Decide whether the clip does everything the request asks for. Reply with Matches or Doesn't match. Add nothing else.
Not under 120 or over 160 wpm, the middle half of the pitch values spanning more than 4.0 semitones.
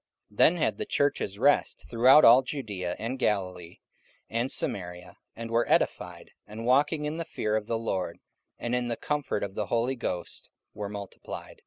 Doesn't match